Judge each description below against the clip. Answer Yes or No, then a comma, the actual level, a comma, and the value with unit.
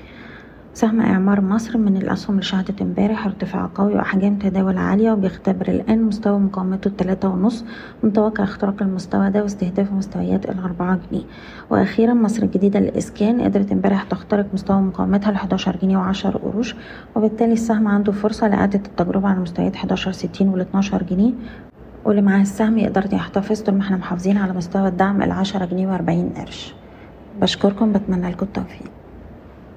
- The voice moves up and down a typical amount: No, narrow, 1.8 semitones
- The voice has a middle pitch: No, high, 200 Hz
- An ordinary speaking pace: No, fast, 150 wpm